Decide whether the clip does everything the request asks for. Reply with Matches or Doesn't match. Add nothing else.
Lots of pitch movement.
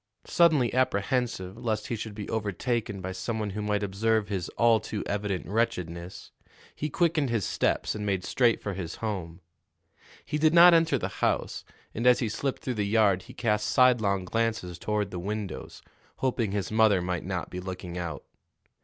Doesn't match